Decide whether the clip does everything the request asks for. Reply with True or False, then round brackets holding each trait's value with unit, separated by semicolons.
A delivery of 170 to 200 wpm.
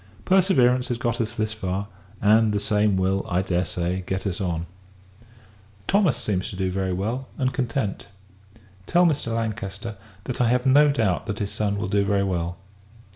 True (180 wpm)